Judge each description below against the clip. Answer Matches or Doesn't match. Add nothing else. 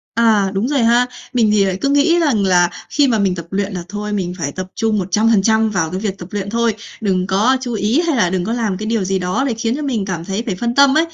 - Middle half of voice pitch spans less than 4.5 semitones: Matches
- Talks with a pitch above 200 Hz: Matches